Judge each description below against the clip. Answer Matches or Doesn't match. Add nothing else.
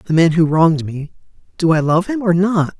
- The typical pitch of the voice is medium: Matches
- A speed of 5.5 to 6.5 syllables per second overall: Matches